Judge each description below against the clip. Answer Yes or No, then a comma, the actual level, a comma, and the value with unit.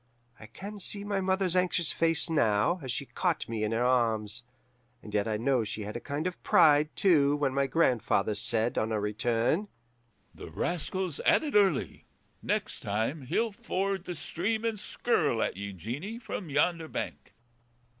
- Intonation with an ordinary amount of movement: No, wide, 8.6 semitones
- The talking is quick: No, average, 175 wpm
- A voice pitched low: No, medium, 145 Hz